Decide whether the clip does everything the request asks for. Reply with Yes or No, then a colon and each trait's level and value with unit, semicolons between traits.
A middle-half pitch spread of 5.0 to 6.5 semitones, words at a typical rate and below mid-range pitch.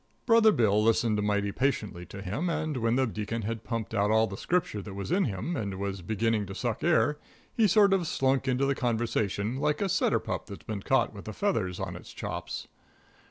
No: average, 5.3 semitones; fast, 210 wpm; low, 115 Hz